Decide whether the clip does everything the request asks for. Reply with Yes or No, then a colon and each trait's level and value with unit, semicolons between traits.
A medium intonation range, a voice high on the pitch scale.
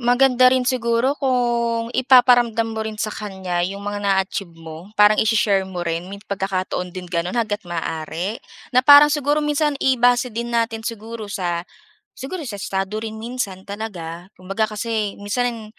Yes: average, 4.2 semitones; high, 220 Hz